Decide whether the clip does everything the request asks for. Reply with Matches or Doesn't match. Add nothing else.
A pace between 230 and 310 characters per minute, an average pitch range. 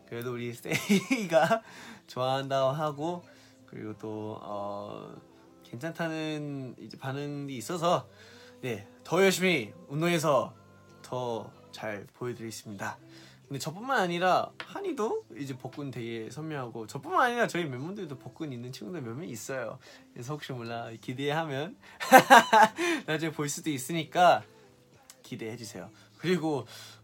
Doesn't match